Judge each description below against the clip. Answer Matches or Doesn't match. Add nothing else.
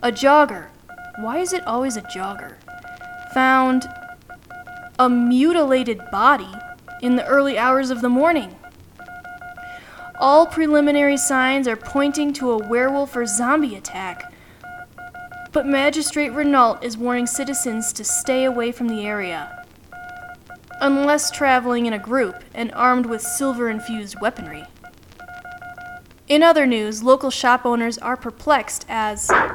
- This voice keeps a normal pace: Doesn't match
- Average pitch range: Doesn't match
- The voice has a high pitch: Matches